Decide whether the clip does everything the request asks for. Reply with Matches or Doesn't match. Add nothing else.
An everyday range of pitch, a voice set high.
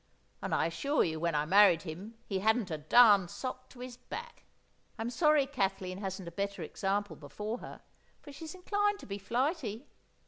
Doesn't match